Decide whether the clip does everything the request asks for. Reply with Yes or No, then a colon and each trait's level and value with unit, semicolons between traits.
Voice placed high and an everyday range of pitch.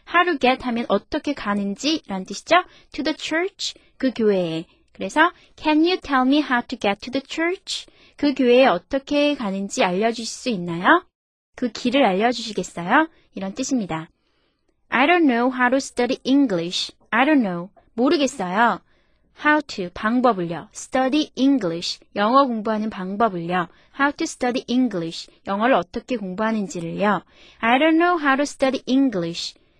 No: very high, 250 Hz; wide, 5.9 semitones